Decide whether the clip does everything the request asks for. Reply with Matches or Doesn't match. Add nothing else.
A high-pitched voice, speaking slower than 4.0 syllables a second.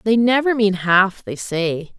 Matches